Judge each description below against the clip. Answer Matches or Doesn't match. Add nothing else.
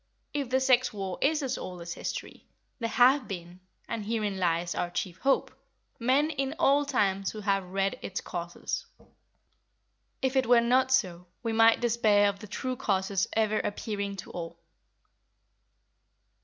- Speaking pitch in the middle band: Doesn't match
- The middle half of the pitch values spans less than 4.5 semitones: Doesn't match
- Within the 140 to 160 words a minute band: Matches